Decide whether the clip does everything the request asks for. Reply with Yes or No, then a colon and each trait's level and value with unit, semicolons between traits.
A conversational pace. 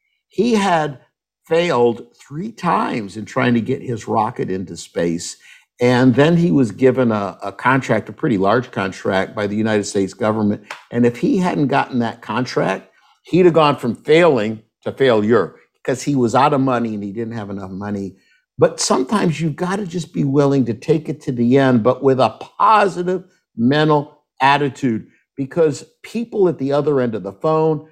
Yes: average, 185 wpm